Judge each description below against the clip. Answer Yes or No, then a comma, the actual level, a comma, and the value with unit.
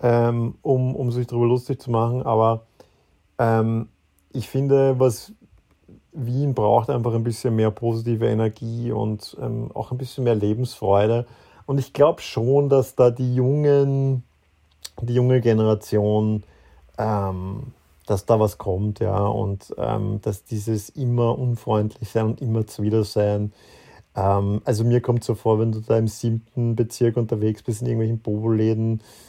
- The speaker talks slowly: No, average, 150 wpm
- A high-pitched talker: No, low, 115 Hz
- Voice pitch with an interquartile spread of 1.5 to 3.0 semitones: Yes, narrow, 2.5 semitones